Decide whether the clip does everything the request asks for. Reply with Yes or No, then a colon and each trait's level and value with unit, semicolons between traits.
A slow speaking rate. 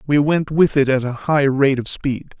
No: fast, 250 wpm